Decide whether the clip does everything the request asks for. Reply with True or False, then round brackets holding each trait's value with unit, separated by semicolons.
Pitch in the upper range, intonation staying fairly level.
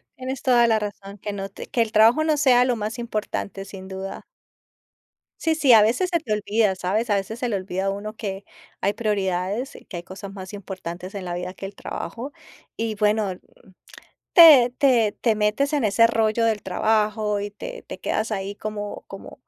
False (210 Hz; 3.1 semitones)